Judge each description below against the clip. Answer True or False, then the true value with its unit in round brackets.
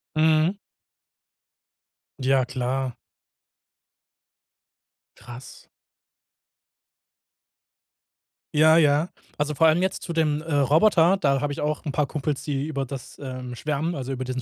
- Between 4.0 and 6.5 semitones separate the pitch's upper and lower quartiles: False (2.9 semitones)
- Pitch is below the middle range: False (145 Hz)